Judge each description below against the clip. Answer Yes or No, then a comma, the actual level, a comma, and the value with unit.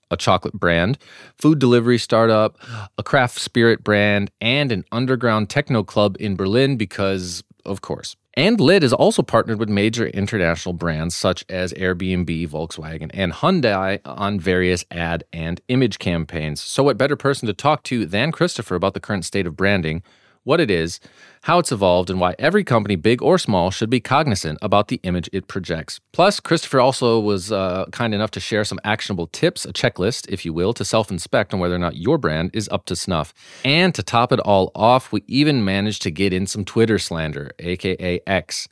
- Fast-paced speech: No, average, 190 wpm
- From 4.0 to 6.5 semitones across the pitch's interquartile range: Yes, average, 4.7 semitones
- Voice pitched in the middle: No, low, 100 Hz